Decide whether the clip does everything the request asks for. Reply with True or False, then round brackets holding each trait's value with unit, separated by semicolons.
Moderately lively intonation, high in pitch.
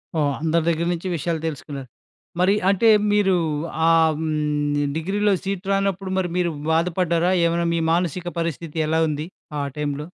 False (3.1 semitones; 165 Hz)